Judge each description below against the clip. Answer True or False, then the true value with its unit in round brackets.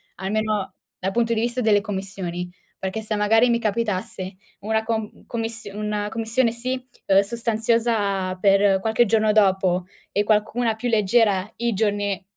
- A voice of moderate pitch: False (215 Hz)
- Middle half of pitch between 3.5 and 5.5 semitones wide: False (2.6 semitones)